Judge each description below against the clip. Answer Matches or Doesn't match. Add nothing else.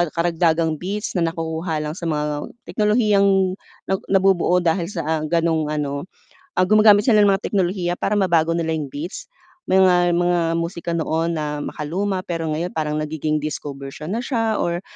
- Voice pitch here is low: Doesn't match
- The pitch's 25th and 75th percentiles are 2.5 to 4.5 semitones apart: Matches